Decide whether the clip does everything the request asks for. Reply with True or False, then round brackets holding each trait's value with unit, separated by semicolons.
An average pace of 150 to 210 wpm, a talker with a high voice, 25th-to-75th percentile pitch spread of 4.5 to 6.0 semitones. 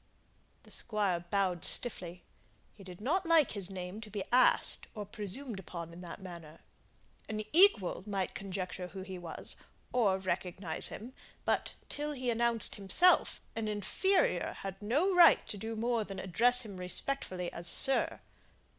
True (155 wpm; 200 Hz; 4.8 semitones)